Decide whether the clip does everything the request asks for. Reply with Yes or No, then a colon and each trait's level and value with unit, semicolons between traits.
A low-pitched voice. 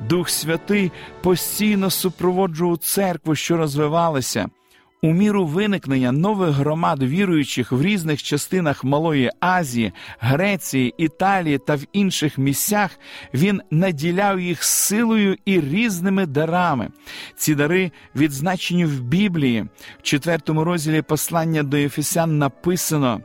No: medium, 165 Hz